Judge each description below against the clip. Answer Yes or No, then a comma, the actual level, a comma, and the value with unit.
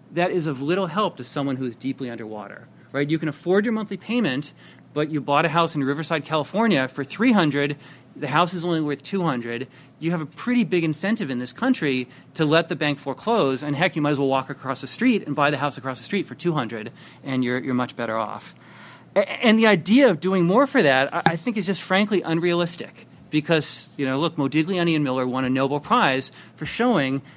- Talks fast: Yes, fast, 230 wpm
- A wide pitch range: No, average, 4.9 semitones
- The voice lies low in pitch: No, medium, 150 Hz